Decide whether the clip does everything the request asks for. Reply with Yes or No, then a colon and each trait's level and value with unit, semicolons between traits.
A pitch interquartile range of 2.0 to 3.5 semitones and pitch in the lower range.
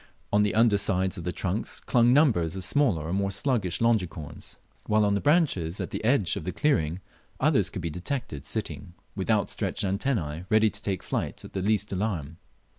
No: average, 4.2 semitones; low, 100 Hz